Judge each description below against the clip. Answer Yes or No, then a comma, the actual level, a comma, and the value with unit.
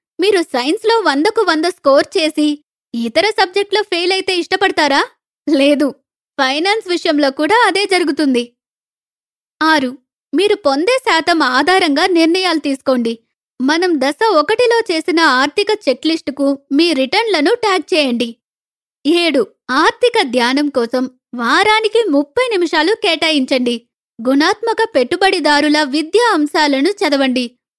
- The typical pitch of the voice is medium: No, very high, 320 Hz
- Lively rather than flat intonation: Yes, wide, 5.7 semitones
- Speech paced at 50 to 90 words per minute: No, average, 100 wpm